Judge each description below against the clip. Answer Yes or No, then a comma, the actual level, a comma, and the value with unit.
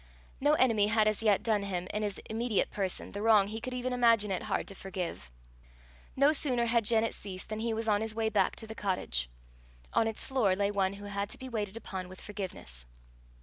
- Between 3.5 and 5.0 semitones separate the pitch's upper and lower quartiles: No, narrow, 2.6 semitones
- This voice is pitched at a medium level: No, high, 210 Hz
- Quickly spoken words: Yes, fast, 220 wpm